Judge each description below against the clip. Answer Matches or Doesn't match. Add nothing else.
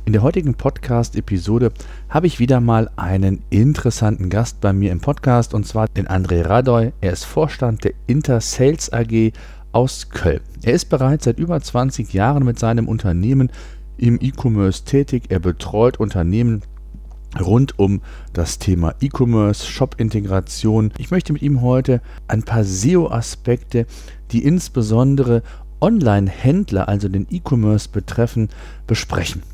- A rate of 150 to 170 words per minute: Doesn't match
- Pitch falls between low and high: Doesn't match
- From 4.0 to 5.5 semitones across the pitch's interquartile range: Matches